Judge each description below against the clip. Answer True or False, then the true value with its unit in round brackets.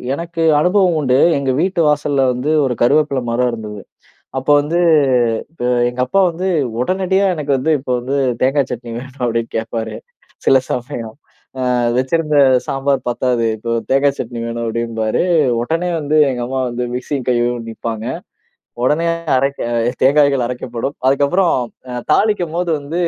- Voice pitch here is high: False (135 Hz)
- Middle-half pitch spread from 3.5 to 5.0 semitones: True (4.1 semitones)